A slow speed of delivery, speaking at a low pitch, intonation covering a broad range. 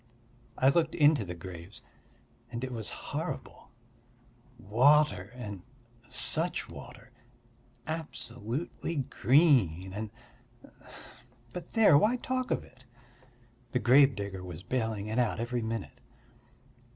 Yes: slow, 105 wpm; low, 120 Hz; wide, 6.0 semitones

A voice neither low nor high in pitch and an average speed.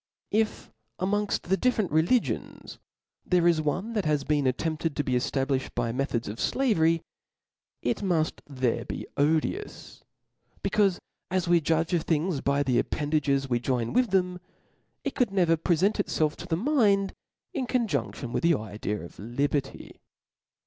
Yes: medium, 160 Hz; average, 155 wpm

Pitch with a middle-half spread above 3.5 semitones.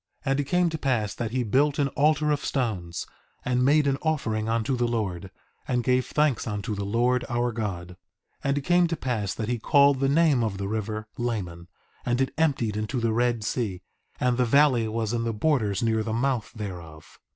Yes: average, 4.2 semitones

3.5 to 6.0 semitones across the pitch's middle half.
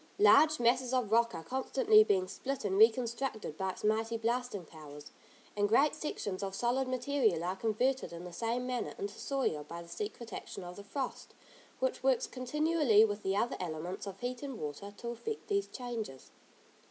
Yes: average, 5.3 semitones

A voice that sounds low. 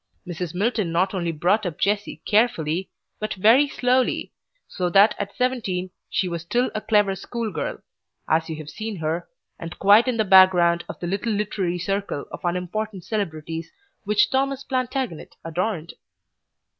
No: high, 195 Hz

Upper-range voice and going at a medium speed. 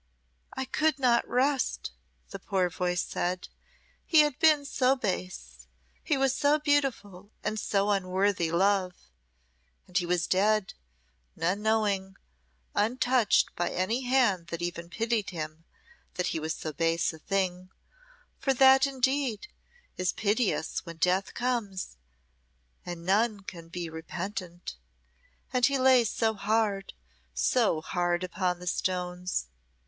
No: high, 195 Hz; slow, 130 wpm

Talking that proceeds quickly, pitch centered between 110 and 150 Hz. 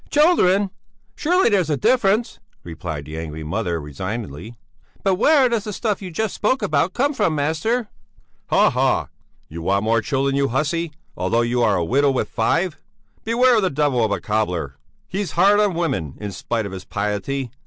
No: average, 175 wpm; medium, 140 Hz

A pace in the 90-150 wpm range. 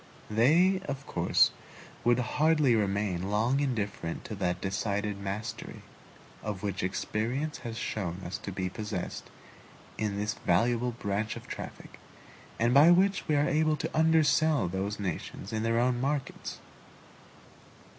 Yes: slow, 135 wpm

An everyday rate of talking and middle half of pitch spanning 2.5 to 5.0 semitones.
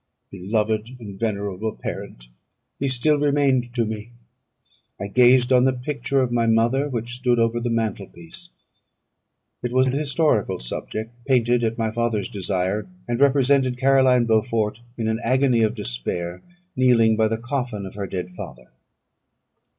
Yes: average, 150 wpm; average, 3.2 semitones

